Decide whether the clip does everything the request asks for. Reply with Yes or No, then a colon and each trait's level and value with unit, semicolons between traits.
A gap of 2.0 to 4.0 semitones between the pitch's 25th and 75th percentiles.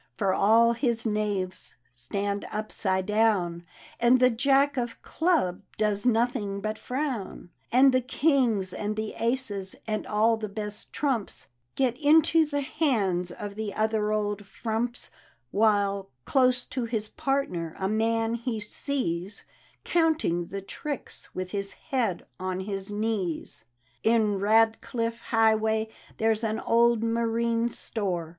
Yes: average, 3.0 semitones